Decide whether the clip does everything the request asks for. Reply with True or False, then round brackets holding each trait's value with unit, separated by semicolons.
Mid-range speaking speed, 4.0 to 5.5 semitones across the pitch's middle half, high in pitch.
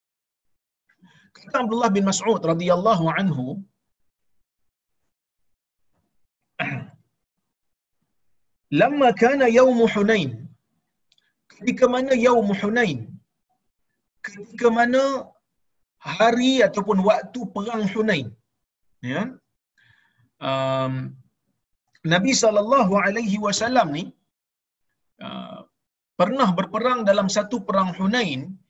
True (75 wpm; 5.1 semitones; 205 Hz)